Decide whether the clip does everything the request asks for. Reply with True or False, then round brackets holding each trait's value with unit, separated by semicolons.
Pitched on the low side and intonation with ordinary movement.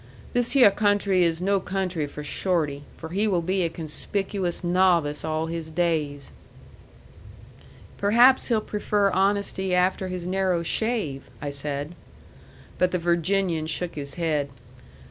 False (180 Hz; 3.7 semitones)